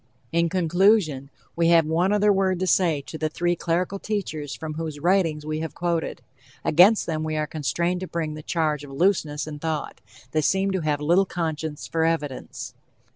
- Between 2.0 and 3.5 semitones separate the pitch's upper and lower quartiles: Yes, average, 2.7 semitones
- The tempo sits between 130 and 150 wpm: No, average, 185 wpm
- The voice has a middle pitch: Yes, medium, 165 Hz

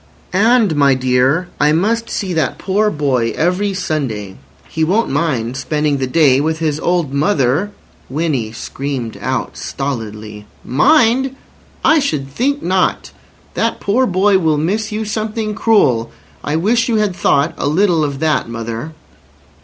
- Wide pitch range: Yes, wide, 7.3 semitones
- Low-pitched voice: No, medium, 160 Hz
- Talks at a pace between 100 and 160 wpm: Yes, average, 145 wpm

